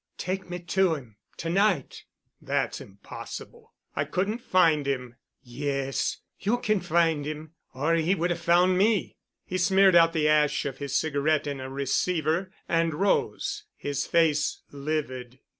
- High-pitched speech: No, medium, 160 Hz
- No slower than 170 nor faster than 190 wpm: No, average, 145 wpm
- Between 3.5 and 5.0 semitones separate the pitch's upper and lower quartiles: Yes, average, 4.3 semitones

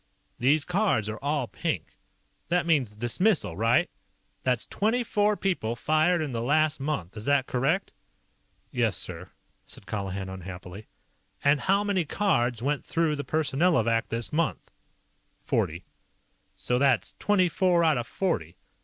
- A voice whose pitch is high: No, medium, 145 Hz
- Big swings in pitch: Yes, wide, 7.1 semitones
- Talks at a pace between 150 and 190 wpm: No, average, 140 wpm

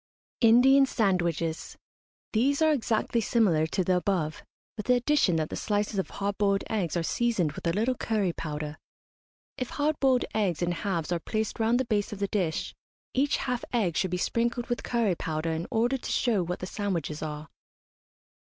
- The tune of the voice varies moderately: No, wide, 5.7 semitones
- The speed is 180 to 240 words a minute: Yes, average, 185 wpm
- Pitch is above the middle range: Yes, high, 205 Hz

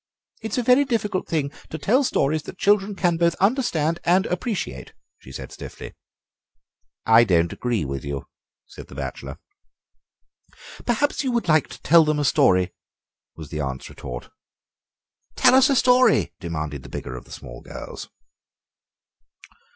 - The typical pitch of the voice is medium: Yes, medium, 160 Hz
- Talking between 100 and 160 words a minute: Yes, average, 150 wpm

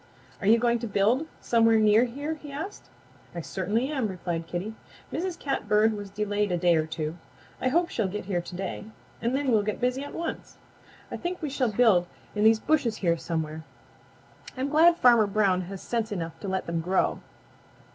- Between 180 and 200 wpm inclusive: Yes, average, 195 wpm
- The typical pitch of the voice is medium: No, high, 215 Hz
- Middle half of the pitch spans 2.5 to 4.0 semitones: No, wide, 5.6 semitones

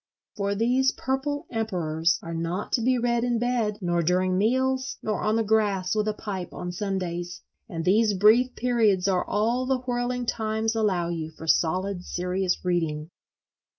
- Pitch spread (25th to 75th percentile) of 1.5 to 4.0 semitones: No, average, 4.9 semitones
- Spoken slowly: No, average, 165 wpm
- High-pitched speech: Yes, high, 205 Hz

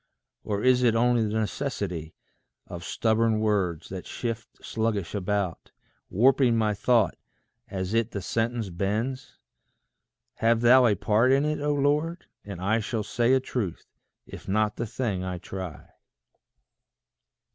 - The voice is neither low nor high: No, low, 110 Hz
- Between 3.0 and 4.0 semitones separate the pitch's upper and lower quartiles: Yes, average, 3.6 semitones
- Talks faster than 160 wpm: No, average, 140 wpm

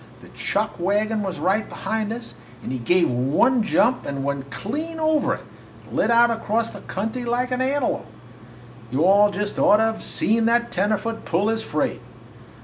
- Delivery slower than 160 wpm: No, average, 175 wpm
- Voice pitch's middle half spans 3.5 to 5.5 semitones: Yes, average, 3.8 semitones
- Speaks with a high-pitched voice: Yes, high, 220 Hz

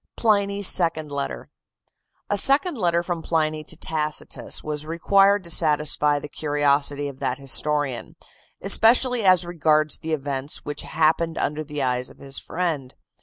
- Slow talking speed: No, average, 155 wpm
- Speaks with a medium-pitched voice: Yes, medium, 155 Hz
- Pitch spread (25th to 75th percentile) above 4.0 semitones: No, average, 3.4 semitones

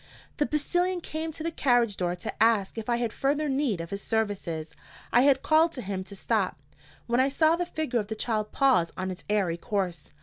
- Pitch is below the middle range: No, high, 235 Hz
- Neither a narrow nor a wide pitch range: No, wide, 6.9 semitones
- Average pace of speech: No, fast, 215 wpm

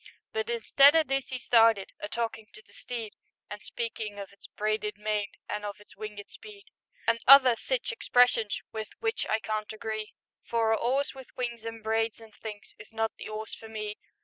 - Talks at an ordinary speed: Yes, average, 195 wpm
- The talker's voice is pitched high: Yes, high, 225 Hz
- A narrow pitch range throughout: Yes, narrow, 2.2 semitones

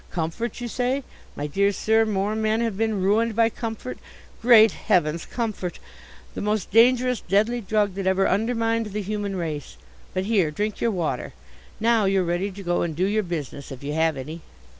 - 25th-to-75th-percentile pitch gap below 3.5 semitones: No, average, 4.3 semitones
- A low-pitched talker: No, high, 205 Hz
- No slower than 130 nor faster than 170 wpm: No, average, 185 wpm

